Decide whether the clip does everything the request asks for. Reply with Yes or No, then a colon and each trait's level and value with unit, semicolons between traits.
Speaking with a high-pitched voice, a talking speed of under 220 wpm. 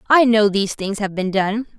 No: high, 210 Hz; fast, 235 wpm